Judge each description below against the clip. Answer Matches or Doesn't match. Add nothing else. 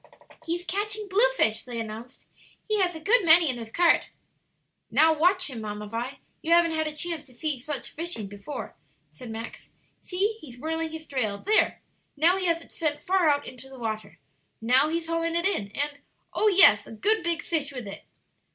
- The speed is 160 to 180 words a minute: Doesn't match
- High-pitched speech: Matches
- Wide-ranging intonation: Matches